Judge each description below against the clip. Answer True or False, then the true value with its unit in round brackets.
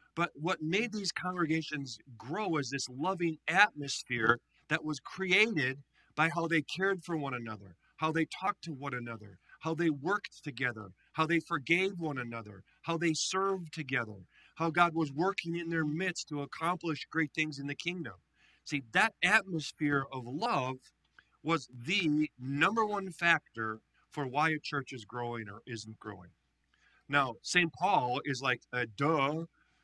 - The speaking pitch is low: False (155 Hz)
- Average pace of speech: True (160 wpm)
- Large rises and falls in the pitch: False (4.7 semitones)